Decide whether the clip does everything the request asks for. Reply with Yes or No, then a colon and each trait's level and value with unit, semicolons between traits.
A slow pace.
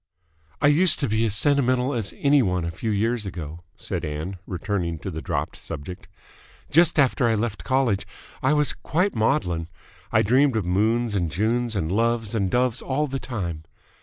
No: average, 180 wpm